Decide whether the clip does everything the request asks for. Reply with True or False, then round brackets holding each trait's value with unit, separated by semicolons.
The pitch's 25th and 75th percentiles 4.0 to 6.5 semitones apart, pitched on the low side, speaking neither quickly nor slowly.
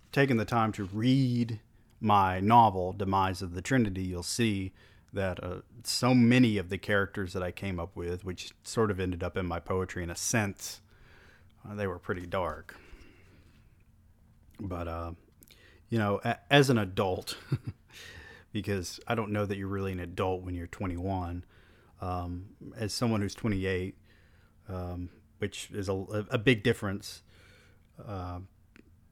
False (3.1 semitones; 100 Hz; 150 wpm)